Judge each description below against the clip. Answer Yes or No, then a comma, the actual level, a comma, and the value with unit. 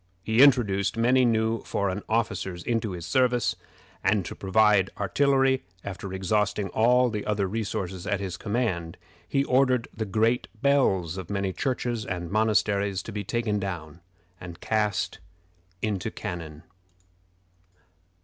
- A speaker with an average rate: No, slow, 130 wpm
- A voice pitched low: Yes, low, 105 Hz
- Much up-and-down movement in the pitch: No, average, 3.5 semitones